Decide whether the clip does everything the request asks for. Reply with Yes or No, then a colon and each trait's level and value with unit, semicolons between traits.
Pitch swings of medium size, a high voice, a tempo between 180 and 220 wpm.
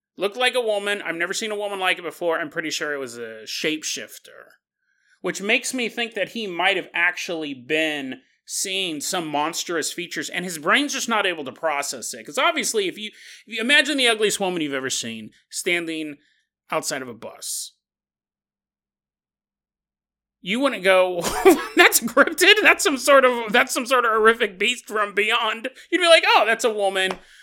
No: wide, 7.1 semitones; high, 205 Hz; average, 185 wpm